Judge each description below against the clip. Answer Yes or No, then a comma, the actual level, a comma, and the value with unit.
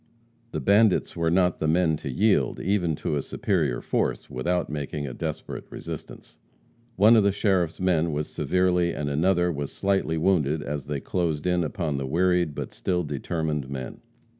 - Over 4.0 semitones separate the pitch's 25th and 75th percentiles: No, average, 3.7 semitones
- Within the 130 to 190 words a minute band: Yes, average, 170 wpm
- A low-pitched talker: Yes, very low, 85 Hz